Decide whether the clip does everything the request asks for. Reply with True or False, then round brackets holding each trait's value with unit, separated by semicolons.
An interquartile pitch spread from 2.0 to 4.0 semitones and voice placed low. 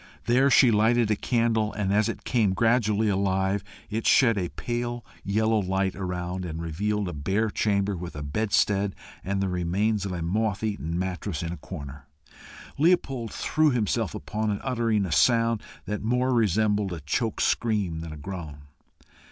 True (3.6 semitones; 105 Hz)